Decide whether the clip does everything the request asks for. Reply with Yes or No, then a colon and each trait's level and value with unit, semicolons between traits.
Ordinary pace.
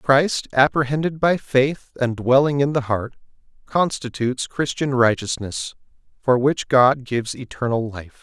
No: slow, 130 wpm